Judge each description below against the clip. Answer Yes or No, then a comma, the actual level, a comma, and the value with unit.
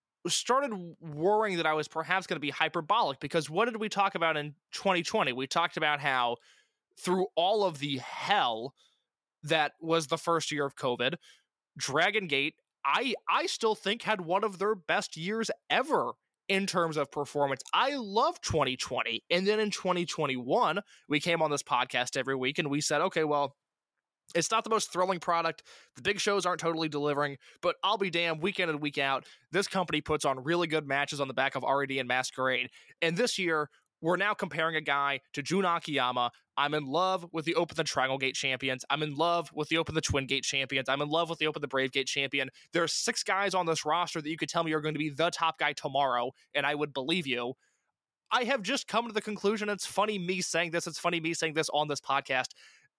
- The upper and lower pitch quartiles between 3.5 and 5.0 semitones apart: Yes, average, 4.5 semitones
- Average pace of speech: No, fast, 215 wpm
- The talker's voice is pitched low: No, medium, 165 Hz